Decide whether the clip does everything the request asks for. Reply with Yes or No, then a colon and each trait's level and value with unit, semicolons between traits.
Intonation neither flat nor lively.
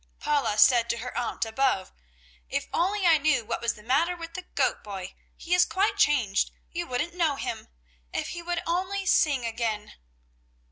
No: wide, 7.0 semitones